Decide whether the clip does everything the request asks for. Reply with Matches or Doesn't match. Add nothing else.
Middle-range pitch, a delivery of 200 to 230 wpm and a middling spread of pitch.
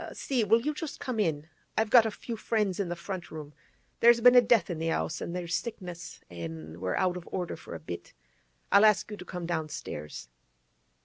Doesn't match